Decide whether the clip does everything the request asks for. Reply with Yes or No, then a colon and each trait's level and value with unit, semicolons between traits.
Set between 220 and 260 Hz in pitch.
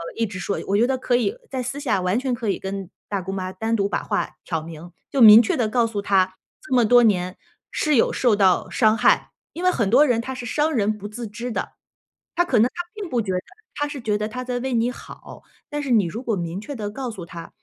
Yes: high, 225 Hz